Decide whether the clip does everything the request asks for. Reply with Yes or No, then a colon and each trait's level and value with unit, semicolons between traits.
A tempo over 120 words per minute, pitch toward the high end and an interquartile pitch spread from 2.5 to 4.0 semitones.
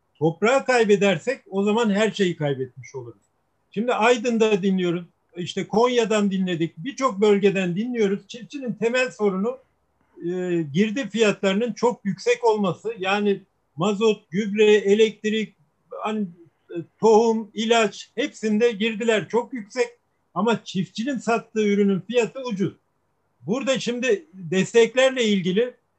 No: average, 110 wpm; high, 210 Hz; average, 3.6 semitones